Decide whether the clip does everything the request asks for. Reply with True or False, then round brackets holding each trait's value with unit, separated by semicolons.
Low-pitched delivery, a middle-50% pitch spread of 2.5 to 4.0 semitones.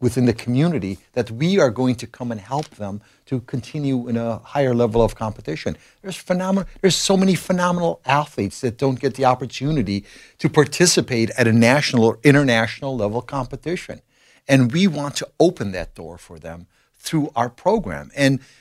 False (130 Hz; 4.6 semitones)